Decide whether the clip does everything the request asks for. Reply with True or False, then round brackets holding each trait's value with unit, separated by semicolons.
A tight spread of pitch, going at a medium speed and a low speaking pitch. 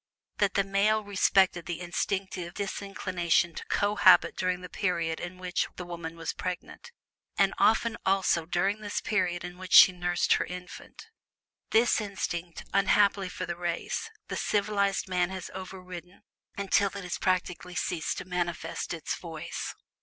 False (2.1 semitones; 150 wpm; 185 Hz)